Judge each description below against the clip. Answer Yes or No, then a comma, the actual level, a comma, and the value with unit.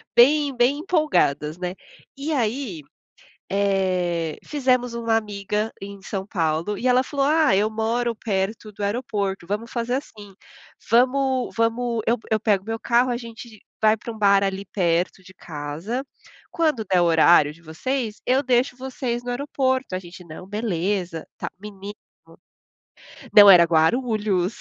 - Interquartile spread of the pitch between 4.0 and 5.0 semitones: Yes, average, 4.6 semitones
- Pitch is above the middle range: Yes, high, 215 Hz